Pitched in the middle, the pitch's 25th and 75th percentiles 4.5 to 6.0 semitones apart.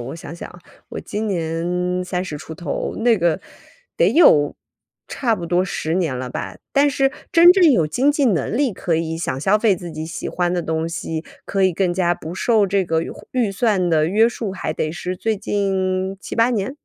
Yes: medium, 180 Hz; average, 4.8 semitones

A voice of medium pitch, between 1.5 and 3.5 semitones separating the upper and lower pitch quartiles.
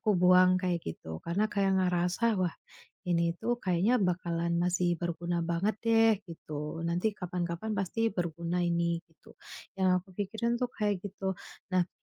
Yes: medium, 180 Hz; average, 2.9 semitones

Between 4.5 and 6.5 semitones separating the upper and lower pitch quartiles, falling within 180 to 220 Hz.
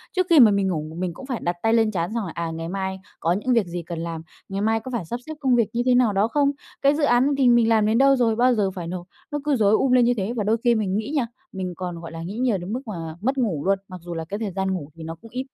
Yes: average, 5.3 semitones; high, 210 Hz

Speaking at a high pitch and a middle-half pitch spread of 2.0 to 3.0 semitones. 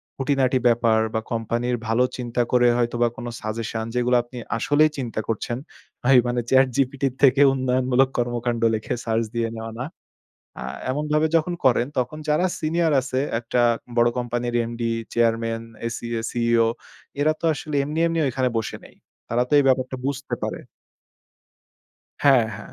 No: low, 125 Hz; narrow, 2.4 semitones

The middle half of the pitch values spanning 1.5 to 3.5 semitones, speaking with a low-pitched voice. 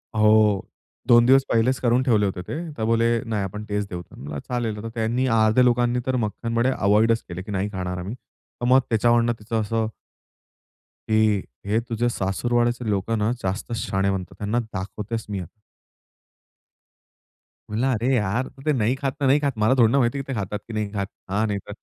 Yes: average, 2.7 semitones; low, 110 Hz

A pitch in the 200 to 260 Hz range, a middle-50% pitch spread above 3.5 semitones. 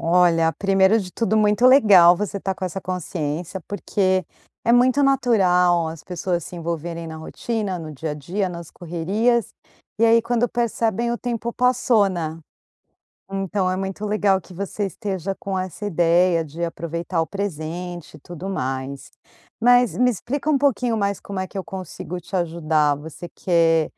No: medium, 185 Hz; average, 4.1 semitones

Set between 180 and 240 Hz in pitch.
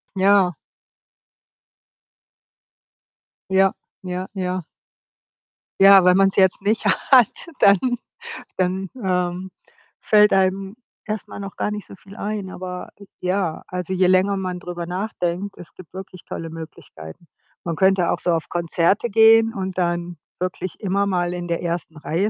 Yes: medium, 185 Hz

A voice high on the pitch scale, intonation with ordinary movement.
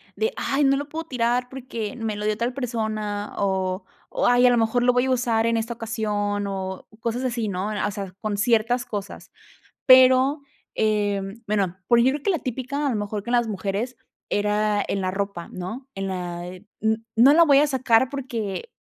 Yes: high, 225 Hz; average, 3.7 semitones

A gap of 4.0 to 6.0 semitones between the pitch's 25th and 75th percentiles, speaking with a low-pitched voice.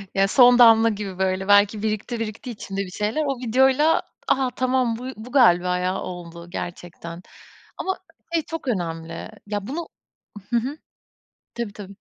No: average, 5.1 semitones; high, 215 Hz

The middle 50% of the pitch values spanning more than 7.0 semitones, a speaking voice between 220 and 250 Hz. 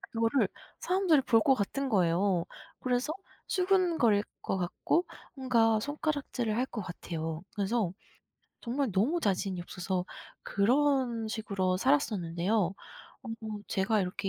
No: wide, 6.0 semitones; high, 225 Hz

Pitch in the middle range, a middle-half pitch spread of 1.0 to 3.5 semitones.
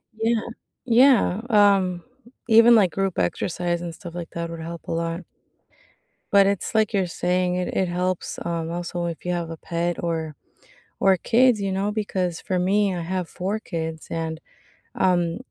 Yes: medium, 180 Hz; average, 2.9 semitones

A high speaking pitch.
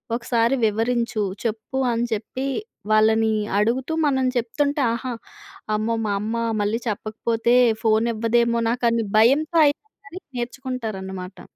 Yes: high, 230 Hz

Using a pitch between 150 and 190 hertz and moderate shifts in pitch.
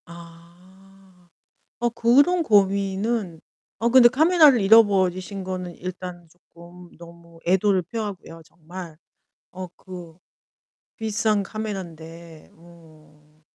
Yes: medium, 185 Hz; average, 3.7 semitones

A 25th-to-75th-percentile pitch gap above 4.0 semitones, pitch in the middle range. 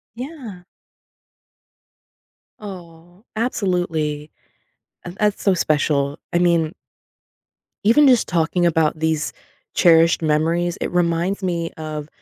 No: average, 2.7 semitones; medium, 170 Hz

